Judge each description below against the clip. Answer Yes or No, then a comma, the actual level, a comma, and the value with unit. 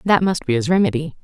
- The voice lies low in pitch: No, medium, 185 Hz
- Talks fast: Yes, fast, 245 wpm